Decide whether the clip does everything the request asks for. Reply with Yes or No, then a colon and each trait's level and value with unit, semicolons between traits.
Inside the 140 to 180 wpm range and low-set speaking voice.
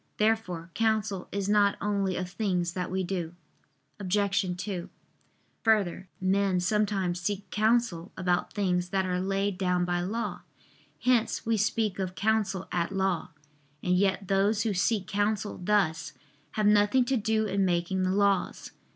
No: average, 150 wpm; high, 195 Hz